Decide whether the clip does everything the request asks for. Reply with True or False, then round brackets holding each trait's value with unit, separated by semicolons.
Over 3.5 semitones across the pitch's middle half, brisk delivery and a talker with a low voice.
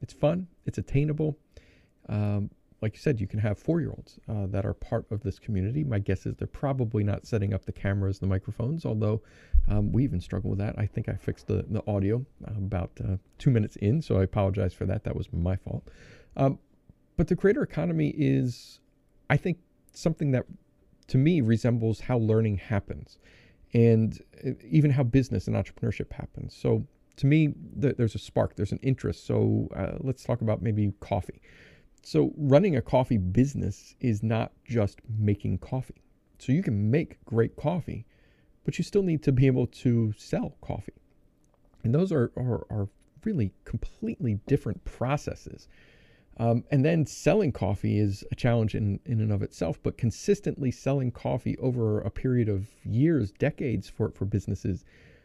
False (5.2 semitones; 175 wpm; 115 Hz)